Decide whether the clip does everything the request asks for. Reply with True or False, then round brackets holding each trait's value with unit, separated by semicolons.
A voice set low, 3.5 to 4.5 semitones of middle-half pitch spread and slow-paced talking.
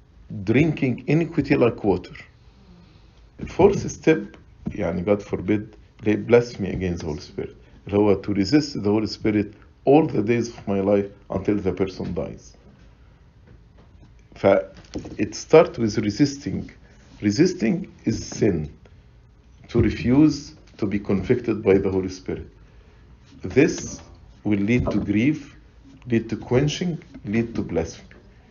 True (105 Hz; 3.8 semitones; 120 wpm)